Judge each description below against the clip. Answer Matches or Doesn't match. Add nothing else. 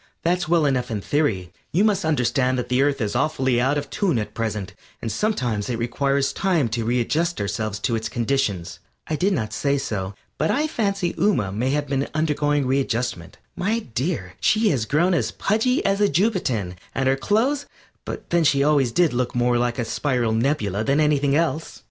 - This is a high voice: Doesn't match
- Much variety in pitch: Matches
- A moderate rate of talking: Matches